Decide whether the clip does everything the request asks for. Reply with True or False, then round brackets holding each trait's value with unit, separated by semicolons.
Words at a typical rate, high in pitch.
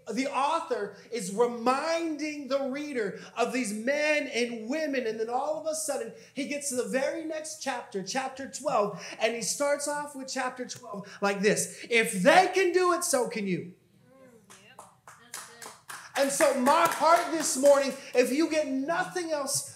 True (165 wpm; 270 Hz)